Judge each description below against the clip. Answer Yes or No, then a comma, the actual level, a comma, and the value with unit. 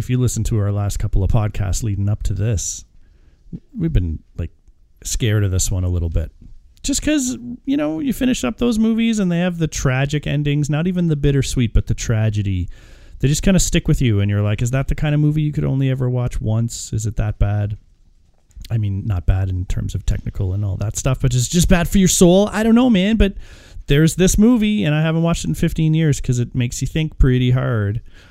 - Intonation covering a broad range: Yes, wide, 8.1 semitones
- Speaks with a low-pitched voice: Yes, low, 125 Hz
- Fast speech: Yes, fast, 240 wpm